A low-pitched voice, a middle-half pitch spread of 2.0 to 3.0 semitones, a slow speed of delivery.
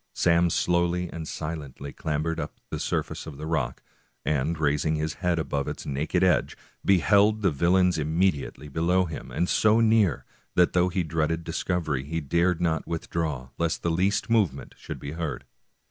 No: very low, 85 Hz; narrow, 2.6 semitones; average, 175 wpm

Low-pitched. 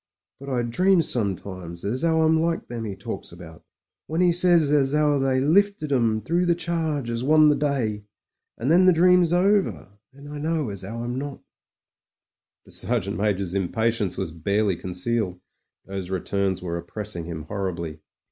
Yes: low, 120 Hz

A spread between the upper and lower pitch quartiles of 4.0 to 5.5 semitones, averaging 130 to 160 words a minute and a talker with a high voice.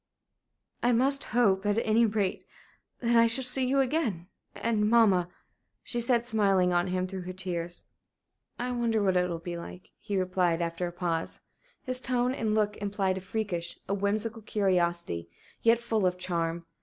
No: average, 4.4 semitones; average, 170 wpm; high, 200 Hz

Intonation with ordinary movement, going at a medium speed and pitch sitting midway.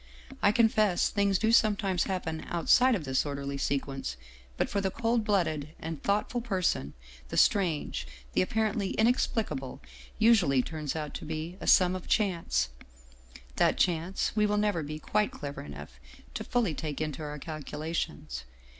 No: wide, 5.9 semitones; average, 160 wpm; medium, 170 Hz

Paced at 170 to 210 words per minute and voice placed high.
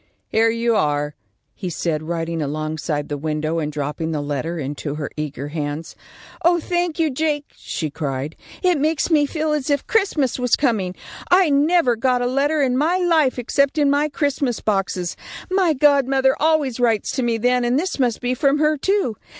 Yes: average, 185 wpm; very high, 250 Hz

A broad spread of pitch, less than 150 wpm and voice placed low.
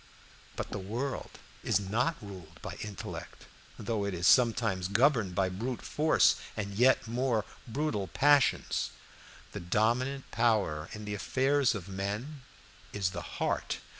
No: average, 4.8 semitones; slow, 135 wpm; low, 110 Hz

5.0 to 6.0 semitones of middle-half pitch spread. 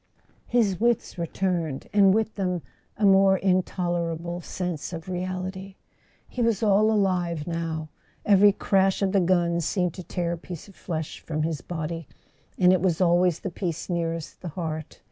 No: narrow, 2.4 semitones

